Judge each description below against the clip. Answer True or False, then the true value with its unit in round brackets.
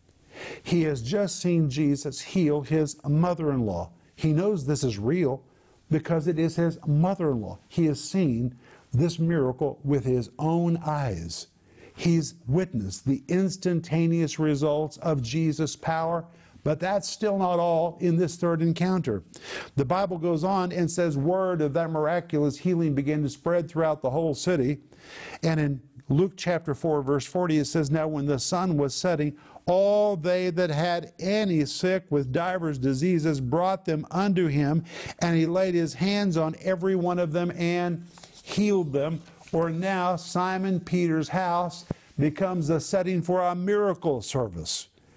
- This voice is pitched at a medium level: True (165 Hz)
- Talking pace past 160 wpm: False (155 wpm)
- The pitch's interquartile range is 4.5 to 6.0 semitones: False (3.3 semitones)